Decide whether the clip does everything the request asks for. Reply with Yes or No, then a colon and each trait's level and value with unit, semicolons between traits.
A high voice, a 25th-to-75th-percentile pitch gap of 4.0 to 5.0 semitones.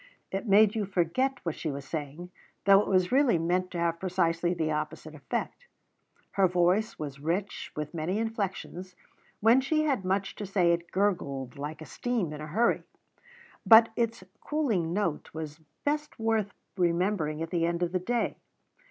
No: medium, 180 Hz; average, 4.5 semitones